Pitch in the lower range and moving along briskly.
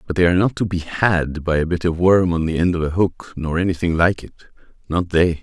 Yes: very low, 85 Hz; fast, 255 wpm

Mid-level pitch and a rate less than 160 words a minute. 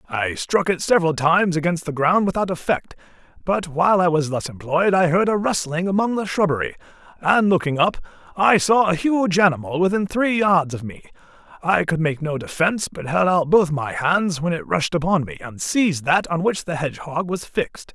No: medium, 170 Hz; fast, 205 wpm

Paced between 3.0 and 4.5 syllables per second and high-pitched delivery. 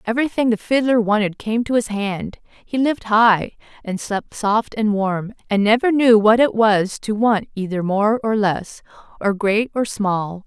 Yes: 4.3 syllables/s; high, 215 Hz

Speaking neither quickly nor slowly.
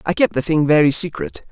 No: fast, 240 wpm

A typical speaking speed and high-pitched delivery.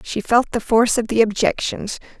Yes: average, 190 wpm; high, 220 Hz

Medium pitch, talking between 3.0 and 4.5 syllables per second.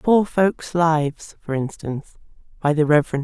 Yes: medium, 160 Hz; 4.2 syllables/s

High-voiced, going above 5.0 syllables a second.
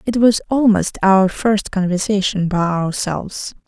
No: high, 195 Hz; 4.2 syllables/s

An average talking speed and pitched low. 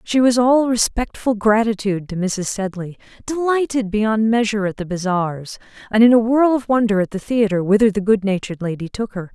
No: average, 185 wpm; high, 215 Hz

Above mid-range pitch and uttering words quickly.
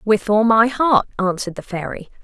No: high, 215 Hz; average, 190 wpm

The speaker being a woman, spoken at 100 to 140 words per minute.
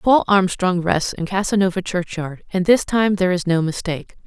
No: female; average, 185 wpm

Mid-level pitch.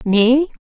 No: very high, 250 Hz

